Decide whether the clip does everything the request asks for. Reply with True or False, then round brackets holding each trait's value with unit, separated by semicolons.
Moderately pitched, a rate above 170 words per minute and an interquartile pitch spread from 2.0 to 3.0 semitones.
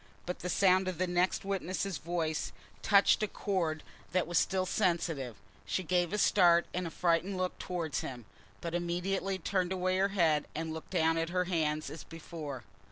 True (175 Hz; 180 wpm; 2.4 semitones)